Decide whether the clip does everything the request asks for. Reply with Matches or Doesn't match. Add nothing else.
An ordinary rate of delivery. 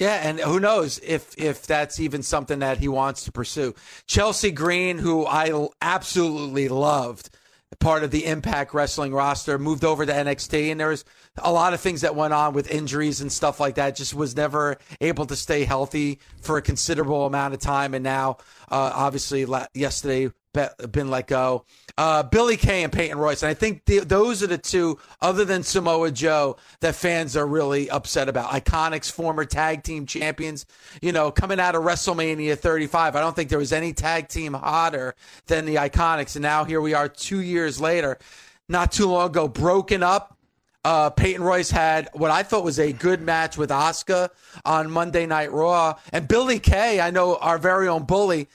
Matches